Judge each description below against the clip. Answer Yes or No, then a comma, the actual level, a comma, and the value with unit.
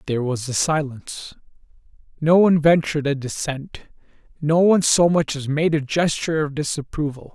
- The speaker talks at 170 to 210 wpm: No, average, 155 wpm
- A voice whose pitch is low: No, medium, 150 Hz